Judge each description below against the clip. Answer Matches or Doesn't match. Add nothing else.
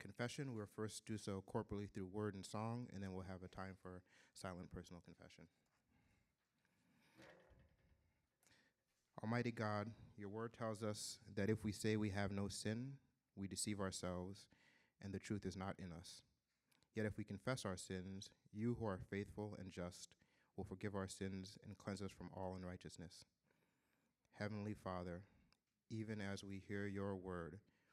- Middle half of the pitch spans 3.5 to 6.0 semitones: Doesn't match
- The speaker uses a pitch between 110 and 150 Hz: Doesn't match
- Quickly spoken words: Doesn't match